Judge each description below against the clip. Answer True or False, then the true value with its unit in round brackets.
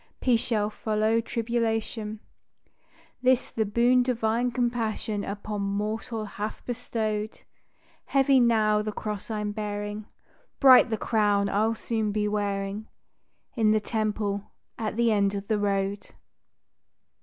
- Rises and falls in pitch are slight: True (1.8 semitones)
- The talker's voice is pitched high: True (215 Hz)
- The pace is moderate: False (120 wpm)